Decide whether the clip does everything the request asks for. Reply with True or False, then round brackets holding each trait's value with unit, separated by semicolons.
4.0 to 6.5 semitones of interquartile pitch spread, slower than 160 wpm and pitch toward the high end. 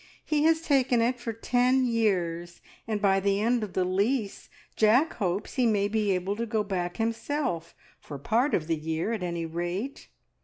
False (5.2 semitones; 185 wpm; 210 Hz)